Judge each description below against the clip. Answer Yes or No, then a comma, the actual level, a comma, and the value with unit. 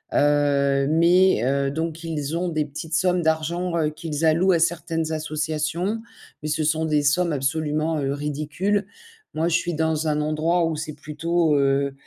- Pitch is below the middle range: No, medium, 155 Hz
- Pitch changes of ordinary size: No, narrow, 2.1 semitones